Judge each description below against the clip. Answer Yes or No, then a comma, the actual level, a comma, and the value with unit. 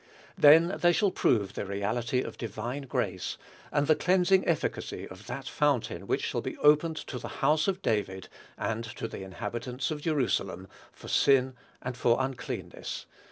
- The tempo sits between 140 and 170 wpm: Yes, average, 160 wpm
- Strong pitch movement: Yes, wide, 5.8 semitones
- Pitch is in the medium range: No, low, 125 Hz